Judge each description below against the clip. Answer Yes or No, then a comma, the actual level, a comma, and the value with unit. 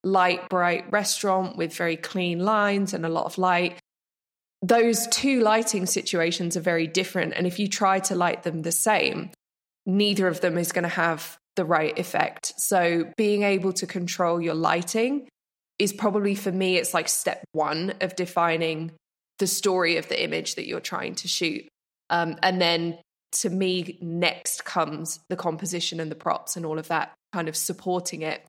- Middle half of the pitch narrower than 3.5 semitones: Yes, narrow, 2.4 semitones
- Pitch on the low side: No, medium, 180 Hz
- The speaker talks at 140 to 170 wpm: No, average, 180 wpm